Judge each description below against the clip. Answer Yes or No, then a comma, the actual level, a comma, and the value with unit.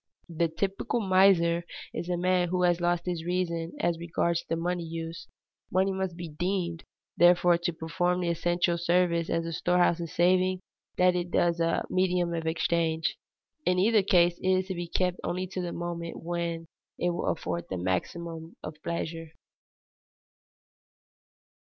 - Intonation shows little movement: Yes, narrow, 1.4 semitones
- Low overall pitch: No, medium, 175 Hz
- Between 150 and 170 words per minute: Yes, average, 165 wpm